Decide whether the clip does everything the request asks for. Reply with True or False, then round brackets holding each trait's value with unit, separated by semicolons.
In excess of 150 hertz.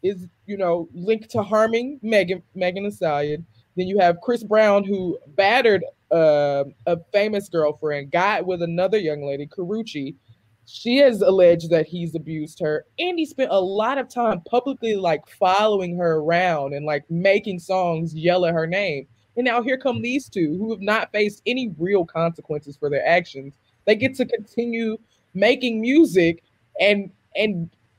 True (185 Hz)